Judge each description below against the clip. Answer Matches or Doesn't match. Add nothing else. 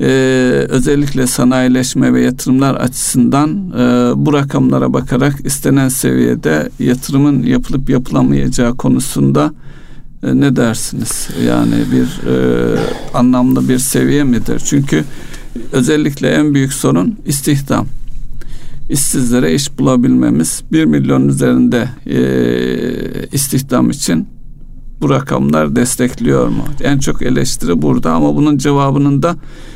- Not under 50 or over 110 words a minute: Matches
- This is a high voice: Doesn't match